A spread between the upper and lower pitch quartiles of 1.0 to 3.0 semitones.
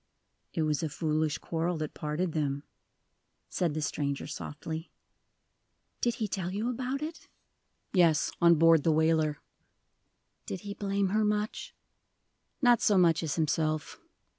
No: average, 4.5 semitones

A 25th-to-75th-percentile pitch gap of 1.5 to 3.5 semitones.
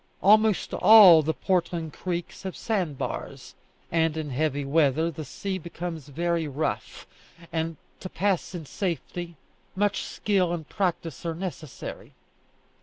Yes: average, 2.9 semitones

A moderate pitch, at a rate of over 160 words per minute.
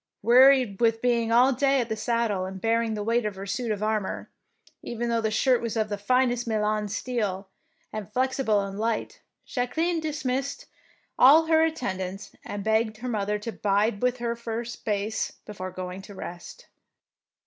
No: high, 225 Hz; average, 180 wpm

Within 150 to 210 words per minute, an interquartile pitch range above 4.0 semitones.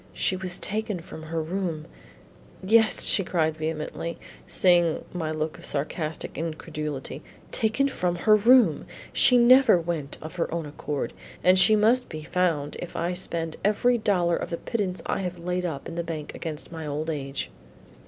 No: average, 175 wpm; average, 3.5 semitones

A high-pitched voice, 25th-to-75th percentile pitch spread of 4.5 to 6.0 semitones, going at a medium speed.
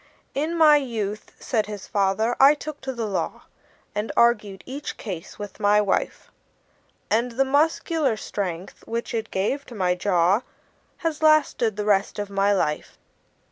Yes: high, 220 Hz; average, 5.2 semitones; average, 155 wpm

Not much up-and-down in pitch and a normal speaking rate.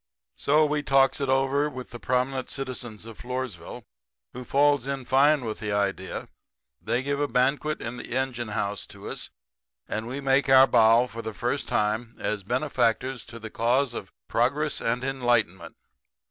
No: average, 3.0 semitones; average, 170 wpm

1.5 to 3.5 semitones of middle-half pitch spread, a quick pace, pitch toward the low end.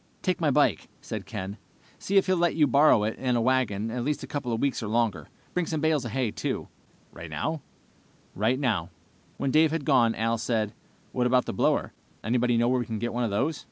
No: average, 4.2 semitones; fast, 230 wpm; low, 125 Hz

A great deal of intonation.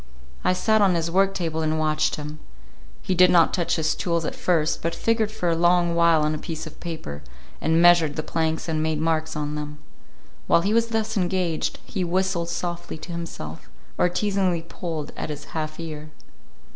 No: narrow, 2.6 semitones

